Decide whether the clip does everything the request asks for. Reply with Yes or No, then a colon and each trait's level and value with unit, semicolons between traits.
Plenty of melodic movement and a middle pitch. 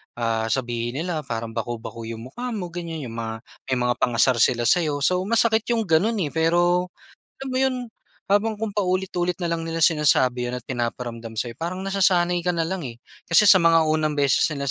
Yes: wide, 7.0 semitones; medium, 160 Hz